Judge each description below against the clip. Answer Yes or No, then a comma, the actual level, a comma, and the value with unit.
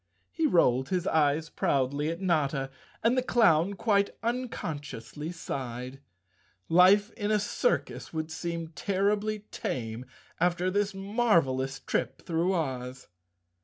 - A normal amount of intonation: No, wide, 6.6 semitones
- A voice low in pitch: No, medium, 170 Hz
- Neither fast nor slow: No, slow, 125 wpm